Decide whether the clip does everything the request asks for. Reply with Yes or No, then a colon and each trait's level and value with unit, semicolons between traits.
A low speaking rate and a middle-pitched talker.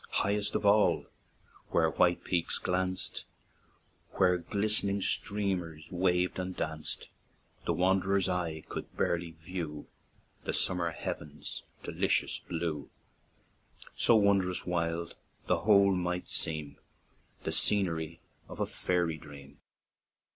No: slow, 110 wpm; very low, 90 Hz